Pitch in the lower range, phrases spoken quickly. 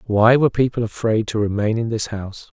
Yes: low, 110 Hz; fast, 210 wpm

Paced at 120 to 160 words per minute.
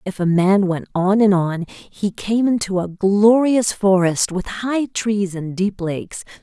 No: average, 175 wpm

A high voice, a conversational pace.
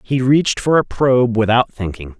No: low, 120 Hz; average, 190 wpm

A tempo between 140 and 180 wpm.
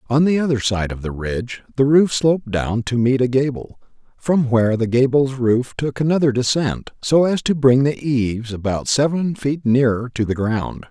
No: average, 200 wpm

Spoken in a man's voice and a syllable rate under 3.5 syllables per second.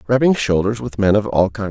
No: male; 5.6 syllables/s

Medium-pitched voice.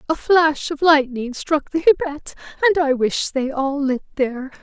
No: very high, 290 Hz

